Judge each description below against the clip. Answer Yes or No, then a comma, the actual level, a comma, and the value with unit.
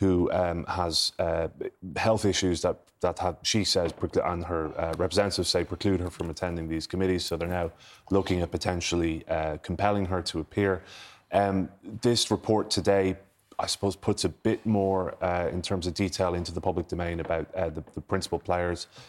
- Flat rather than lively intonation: Yes, narrow, 2.2 semitones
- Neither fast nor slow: Yes, average, 180 wpm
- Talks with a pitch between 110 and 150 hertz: No, very low, 90 Hz